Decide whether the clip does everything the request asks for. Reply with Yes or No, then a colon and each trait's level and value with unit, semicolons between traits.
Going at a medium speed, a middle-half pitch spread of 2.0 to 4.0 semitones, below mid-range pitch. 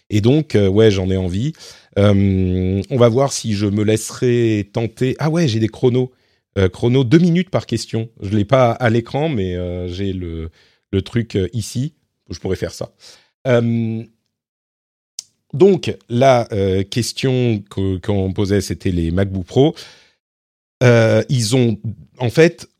No: average, 160 wpm; average, 4.5 semitones; low, 110 Hz